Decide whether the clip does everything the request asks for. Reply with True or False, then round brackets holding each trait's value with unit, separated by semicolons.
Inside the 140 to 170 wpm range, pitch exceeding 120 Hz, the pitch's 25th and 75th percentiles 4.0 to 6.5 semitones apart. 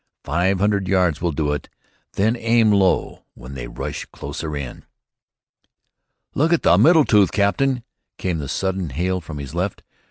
False (160 wpm; 95 Hz; 5.3 semitones)